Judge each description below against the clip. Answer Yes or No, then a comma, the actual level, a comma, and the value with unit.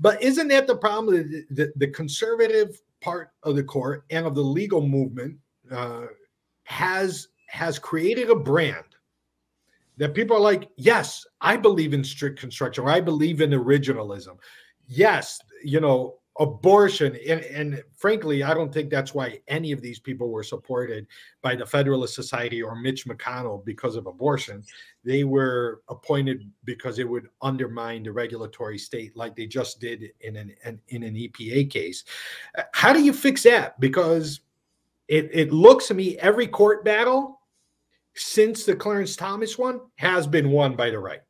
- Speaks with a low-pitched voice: No, medium, 145 Hz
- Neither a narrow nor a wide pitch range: No, wide, 7.2 semitones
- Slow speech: No, average, 165 wpm